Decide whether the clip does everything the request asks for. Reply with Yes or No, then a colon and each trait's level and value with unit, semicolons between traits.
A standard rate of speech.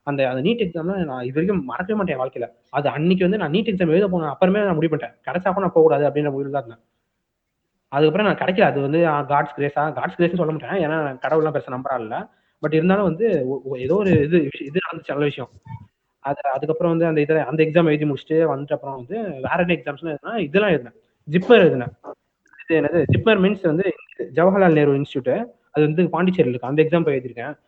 No: fast, 160 wpm